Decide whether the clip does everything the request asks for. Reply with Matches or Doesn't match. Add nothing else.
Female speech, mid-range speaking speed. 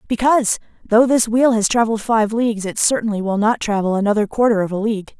Doesn't match